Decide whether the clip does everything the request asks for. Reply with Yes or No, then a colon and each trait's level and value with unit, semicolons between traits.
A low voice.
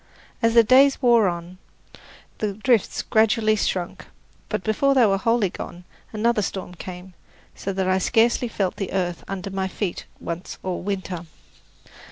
No: high, 195 Hz